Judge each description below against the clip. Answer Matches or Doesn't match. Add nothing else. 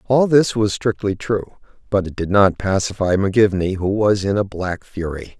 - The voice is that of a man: Matches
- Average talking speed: Matches